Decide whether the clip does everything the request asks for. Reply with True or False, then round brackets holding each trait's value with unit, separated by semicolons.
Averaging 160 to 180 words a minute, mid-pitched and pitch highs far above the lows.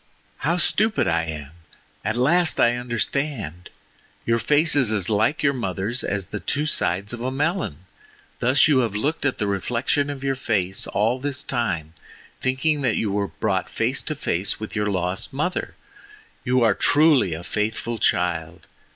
False (165 wpm; 115 Hz; 6.2 semitones)